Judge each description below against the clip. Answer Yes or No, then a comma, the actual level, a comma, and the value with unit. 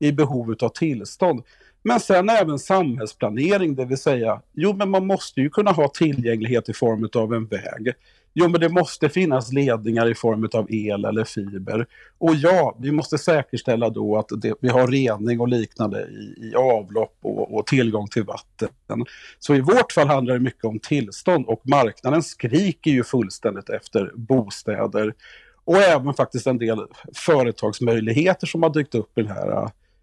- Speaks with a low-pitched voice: Yes, low, 125 Hz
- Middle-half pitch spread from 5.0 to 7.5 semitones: Yes, wide, 5.5 semitones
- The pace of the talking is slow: No, average, 170 wpm